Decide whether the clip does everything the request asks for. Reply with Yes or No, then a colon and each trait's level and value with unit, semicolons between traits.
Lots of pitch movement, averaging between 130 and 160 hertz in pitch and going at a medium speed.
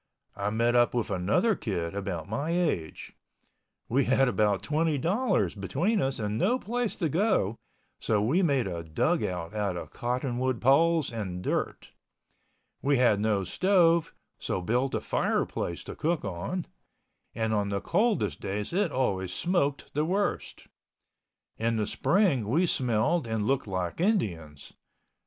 No: wide, 8.8 semitones; low, 120 Hz; average, 145 wpm